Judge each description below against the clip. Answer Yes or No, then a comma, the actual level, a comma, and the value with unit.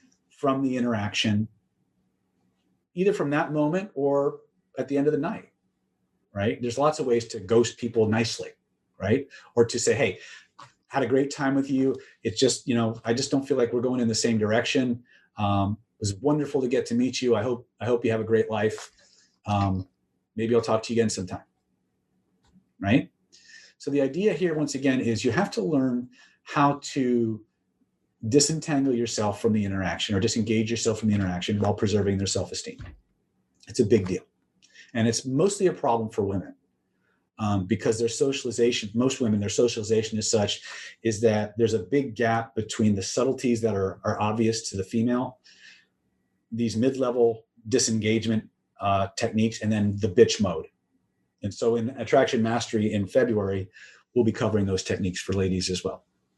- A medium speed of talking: Yes, average, 180 wpm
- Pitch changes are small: No, average, 3.2 semitones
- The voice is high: No, low, 115 Hz